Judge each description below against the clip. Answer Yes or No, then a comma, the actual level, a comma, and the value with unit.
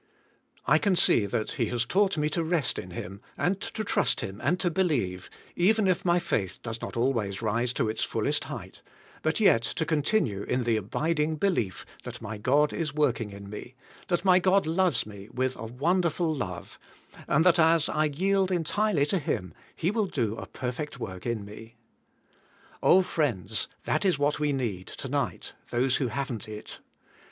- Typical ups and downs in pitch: No, wide, 7.5 semitones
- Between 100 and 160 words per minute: No, average, 185 wpm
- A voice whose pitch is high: No, medium, 140 Hz